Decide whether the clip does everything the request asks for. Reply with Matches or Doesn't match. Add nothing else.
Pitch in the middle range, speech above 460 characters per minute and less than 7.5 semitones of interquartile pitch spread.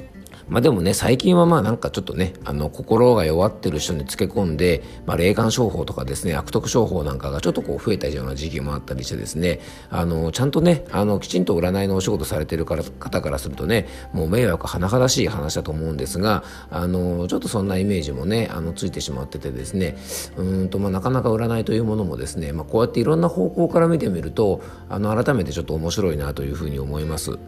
Doesn't match